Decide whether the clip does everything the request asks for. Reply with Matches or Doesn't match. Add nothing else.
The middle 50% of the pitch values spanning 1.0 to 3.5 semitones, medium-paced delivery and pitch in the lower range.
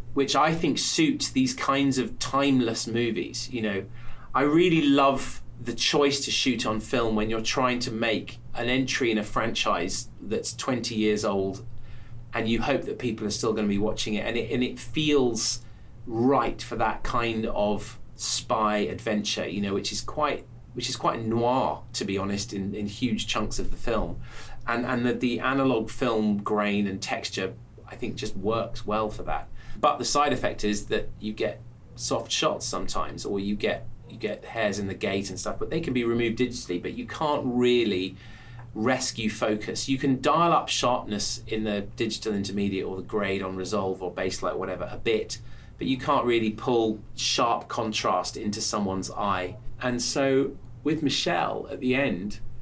Matches